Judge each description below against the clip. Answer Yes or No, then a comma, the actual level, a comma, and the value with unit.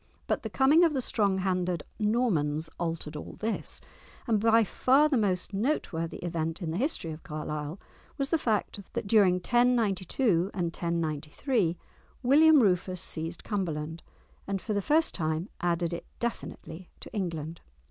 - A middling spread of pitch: No, wide, 5.7 semitones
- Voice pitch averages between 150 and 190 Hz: Yes, medium, 185 Hz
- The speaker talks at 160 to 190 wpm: No, average, 150 wpm